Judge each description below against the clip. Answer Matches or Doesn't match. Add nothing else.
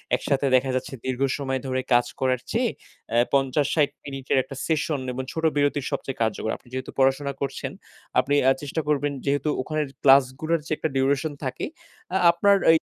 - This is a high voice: Doesn't match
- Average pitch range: Doesn't match